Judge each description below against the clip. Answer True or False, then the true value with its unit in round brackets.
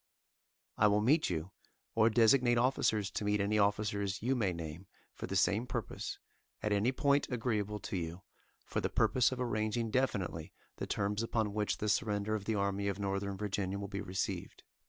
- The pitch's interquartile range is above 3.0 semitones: False (2.4 semitones)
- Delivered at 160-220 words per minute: True (180 wpm)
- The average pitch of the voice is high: False (105 Hz)